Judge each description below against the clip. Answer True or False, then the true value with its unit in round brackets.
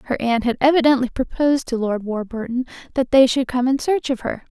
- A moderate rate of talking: False (210 wpm)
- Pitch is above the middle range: True (255 Hz)